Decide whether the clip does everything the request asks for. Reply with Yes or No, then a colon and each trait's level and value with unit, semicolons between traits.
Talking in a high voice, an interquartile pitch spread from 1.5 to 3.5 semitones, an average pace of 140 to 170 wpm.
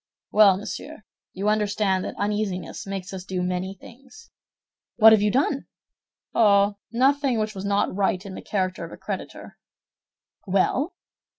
Yes: high, 205 Hz; narrow, 2.6 semitones; average, 150 wpm